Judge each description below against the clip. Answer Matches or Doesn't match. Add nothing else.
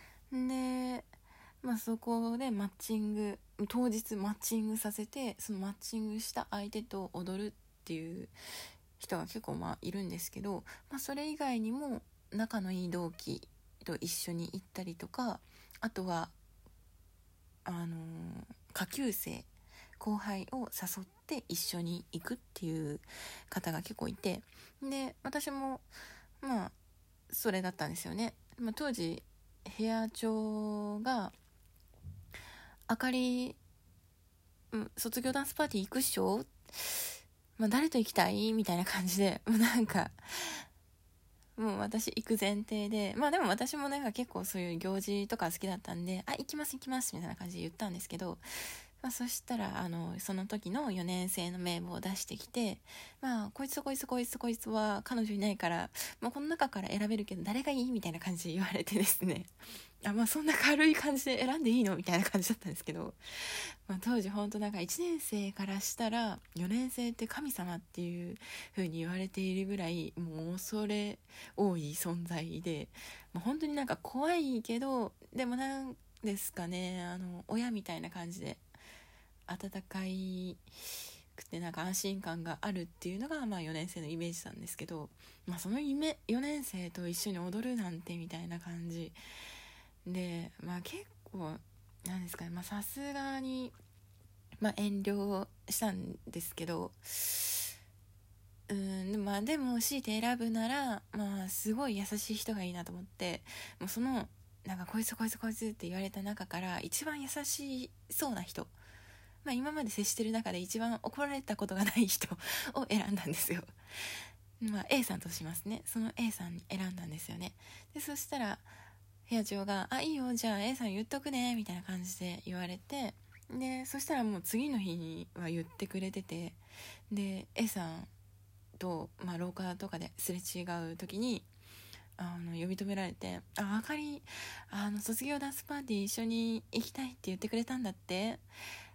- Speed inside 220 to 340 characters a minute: Matches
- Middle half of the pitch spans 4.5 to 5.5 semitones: Matches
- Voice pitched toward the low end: Doesn't match